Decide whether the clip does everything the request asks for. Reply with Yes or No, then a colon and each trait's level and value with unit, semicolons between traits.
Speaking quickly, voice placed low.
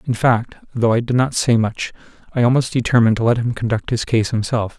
Yes: fast, 225 wpm; low, 120 Hz